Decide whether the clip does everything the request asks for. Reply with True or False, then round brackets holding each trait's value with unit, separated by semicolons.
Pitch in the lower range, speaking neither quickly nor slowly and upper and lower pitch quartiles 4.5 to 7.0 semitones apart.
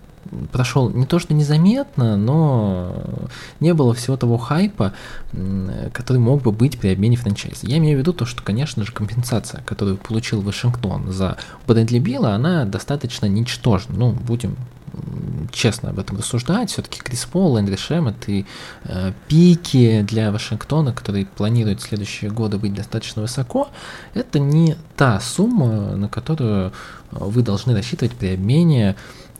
True (120 Hz; 145 wpm; 5.4 semitones)